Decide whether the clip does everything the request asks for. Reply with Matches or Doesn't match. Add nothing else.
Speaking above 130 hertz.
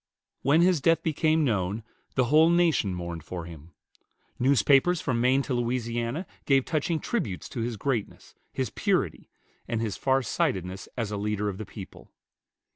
Doesn't match